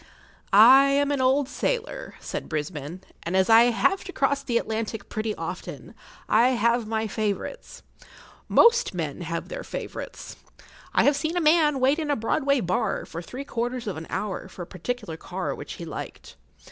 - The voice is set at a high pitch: Yes, high, 235 Hz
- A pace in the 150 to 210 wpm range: Yes, average, 175 wpm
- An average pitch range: No, wide, 6.2 semitones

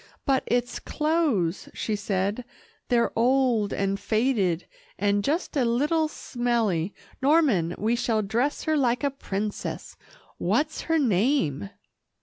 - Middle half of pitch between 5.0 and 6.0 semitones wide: Yes, wide, 5.4 semitones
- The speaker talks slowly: Yes, slow, 125 wpm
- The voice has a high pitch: Yes, high, 235 Hz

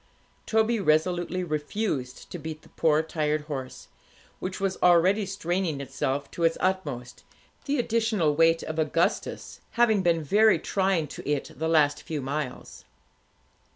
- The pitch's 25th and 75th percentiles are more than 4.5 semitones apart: No, average, 4.2 semitones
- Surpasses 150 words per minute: No, average, 140 wpm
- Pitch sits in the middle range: Yes, medium, 165 Hz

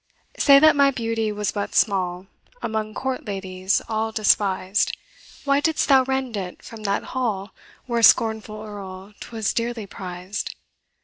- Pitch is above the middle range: Yes, high, 215 Hz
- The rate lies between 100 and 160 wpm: Yes, average, 140 wpm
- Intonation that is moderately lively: Yes, average, 3.5 semitones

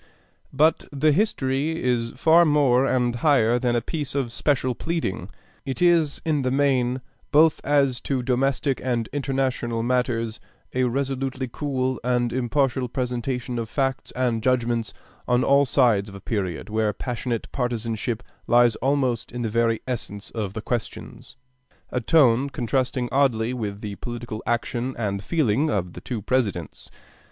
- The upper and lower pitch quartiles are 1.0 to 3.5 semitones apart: Yes, average, 2.8 semitones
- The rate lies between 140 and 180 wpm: Yes, average, 150 wpm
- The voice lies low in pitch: Yes, low, 125 Hz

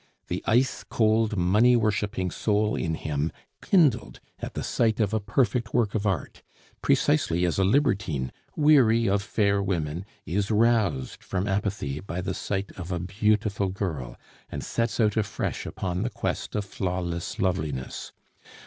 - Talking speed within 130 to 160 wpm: Yes, average, 150 wpm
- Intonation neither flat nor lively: Yes, average, 3.7 semitones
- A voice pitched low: Yes, low, 100 Hz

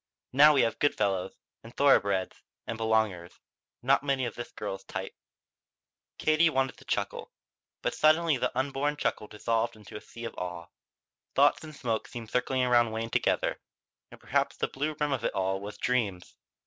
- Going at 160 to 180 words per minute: Yes, average, 175 wpm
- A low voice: Yes, low, 120 Hz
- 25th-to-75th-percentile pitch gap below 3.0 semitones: No, average, 4.7 semitones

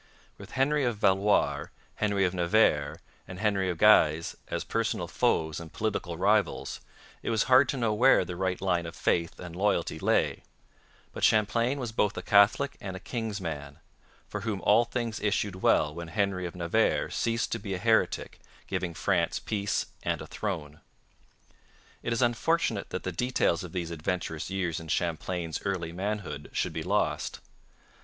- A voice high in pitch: No, very low, 95 Hz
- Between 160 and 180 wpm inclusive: Yes, average, 170 wpm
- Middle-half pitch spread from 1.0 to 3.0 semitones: No, average, 4.3 semitones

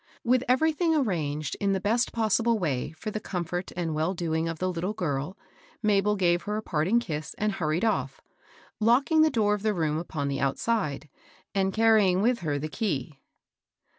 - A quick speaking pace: No, average, 180 wpm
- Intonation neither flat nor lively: No, wide, 5.7 semitones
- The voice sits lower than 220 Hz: Yes, high, 190 Hz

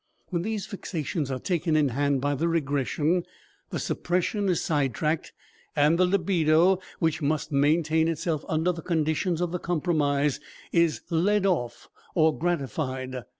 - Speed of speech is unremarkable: Yes, average, 150 wpm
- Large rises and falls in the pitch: No, average, 3.3 semitones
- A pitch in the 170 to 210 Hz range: No, medium, 160 Hz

